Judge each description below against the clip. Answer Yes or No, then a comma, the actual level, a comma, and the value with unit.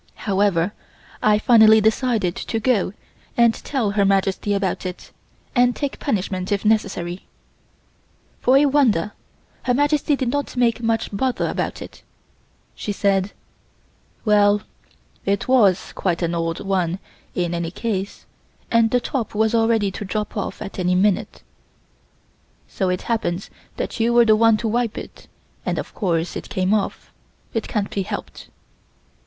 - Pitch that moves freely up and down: No, average, 3.4 semitones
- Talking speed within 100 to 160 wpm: Yes, average, 150 wpm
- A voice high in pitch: Yes, high, 210 Hz